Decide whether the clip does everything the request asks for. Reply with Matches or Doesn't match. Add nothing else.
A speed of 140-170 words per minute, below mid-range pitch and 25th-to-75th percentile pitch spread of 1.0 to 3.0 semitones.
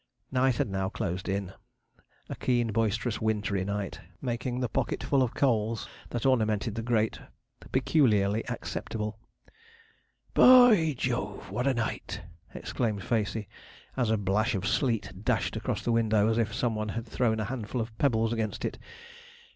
Matches